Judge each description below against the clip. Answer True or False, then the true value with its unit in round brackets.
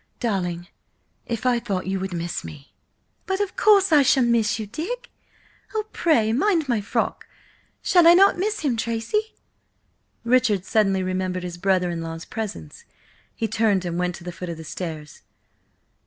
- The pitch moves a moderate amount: False (7.6 semitones)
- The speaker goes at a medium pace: True (165 wpm)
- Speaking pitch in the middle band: False (215 Hz)